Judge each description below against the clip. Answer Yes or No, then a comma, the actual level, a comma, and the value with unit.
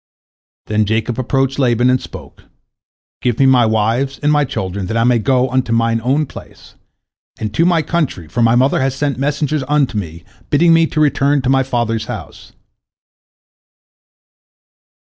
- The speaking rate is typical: Yes, average, 165 wpm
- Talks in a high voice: No, low, 130 Hz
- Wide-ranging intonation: No, average, 3.8 semitones